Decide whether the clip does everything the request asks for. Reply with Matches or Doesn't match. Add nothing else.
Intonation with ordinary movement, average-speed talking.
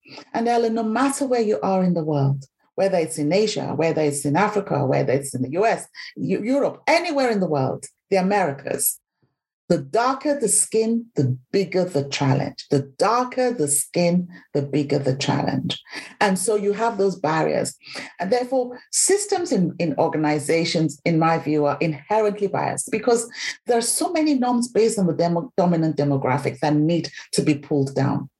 Doesn't match